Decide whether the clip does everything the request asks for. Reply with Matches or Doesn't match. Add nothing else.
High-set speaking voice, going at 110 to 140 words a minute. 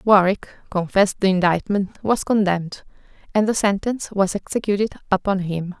Matches